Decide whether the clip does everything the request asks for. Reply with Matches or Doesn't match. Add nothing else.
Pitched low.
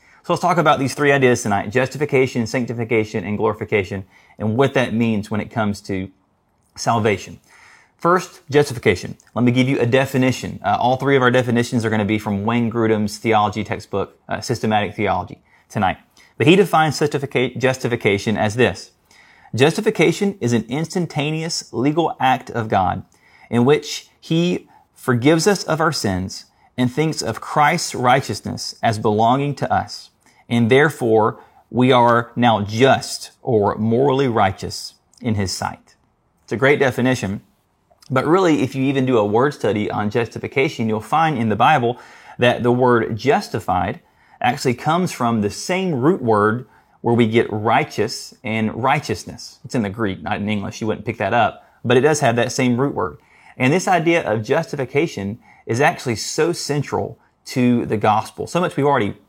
Matches